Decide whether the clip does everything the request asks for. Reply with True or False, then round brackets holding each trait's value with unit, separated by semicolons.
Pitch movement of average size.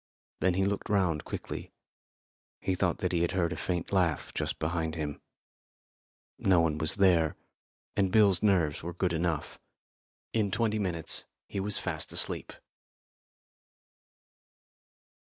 True (3.0 semitones)